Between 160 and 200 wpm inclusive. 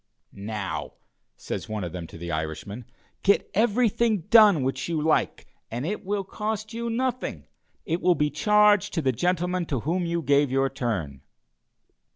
Yes: average, 165 wpm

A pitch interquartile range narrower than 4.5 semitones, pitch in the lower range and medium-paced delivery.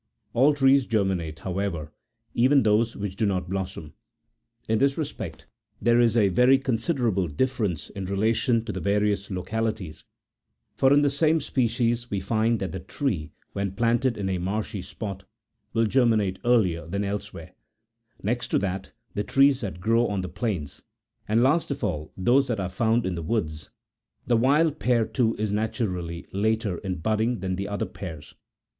Yes: average, 4.1 semitones; low, 105 Hz; average, 170 wpm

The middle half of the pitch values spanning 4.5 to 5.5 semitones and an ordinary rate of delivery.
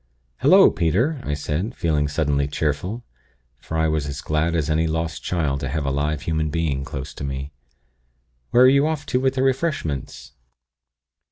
Yes: average, 4.8 semitones; average, 175 wpm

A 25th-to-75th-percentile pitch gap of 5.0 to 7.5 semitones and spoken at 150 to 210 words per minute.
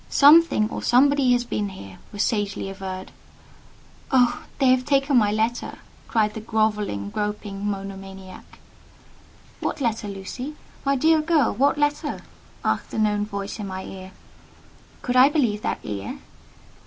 No: average, 5.3 semitones; average, 140 wpm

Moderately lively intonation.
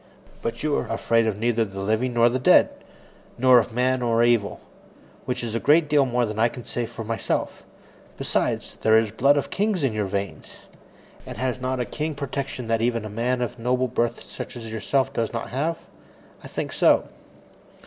No: narrow, 2.3 semitones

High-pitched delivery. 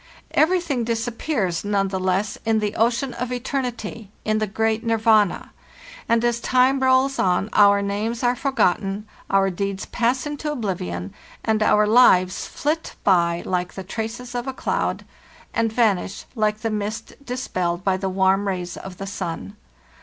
Yes: high, 215 Hz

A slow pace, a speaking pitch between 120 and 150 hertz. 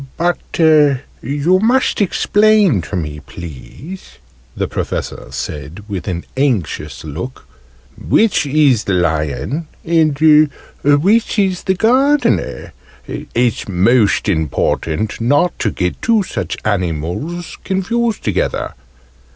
Yes: slow, 105 wpm; low, 135 Hz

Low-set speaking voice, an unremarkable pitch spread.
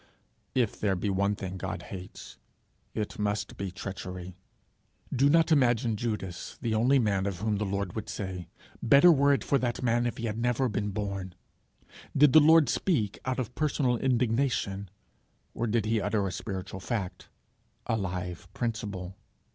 Yes: low, 110 Hz; average, 4.1 semitones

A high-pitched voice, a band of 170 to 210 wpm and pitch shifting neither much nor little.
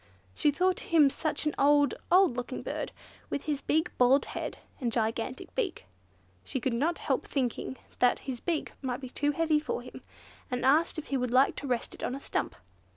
Yes: very high, 275 Hz; average, 200 wpm; average, 3.6 semitones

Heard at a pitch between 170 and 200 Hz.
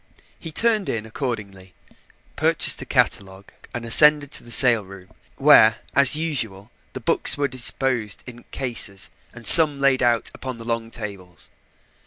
No: low, 120 Hz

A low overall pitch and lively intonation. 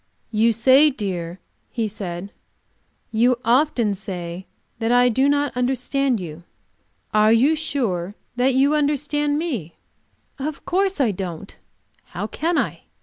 No: high, 245 Hz; wide, 6.2 semitones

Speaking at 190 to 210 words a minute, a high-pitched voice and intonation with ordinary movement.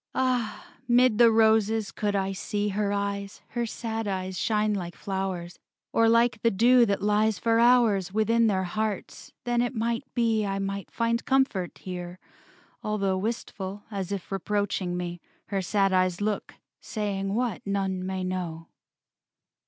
No: average, 150 wpm; high, 205 Hz; average, 3.0 semitones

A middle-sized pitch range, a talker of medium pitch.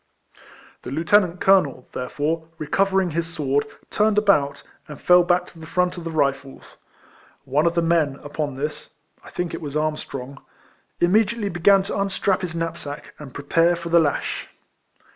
Yes: average, 3.7 semitones; medium, 165 Hz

